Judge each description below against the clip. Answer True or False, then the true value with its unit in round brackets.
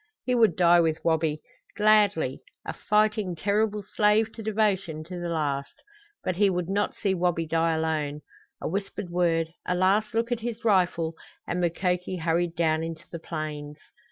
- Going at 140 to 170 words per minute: True (165 wpm)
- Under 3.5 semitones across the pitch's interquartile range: False (4.2 semitones)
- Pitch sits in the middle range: True (175 Hz)